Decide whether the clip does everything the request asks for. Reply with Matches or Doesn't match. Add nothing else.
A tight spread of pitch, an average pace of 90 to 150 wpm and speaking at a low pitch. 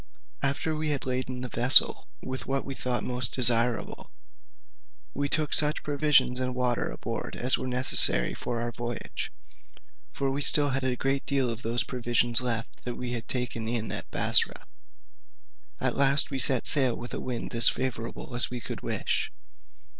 Doesn't match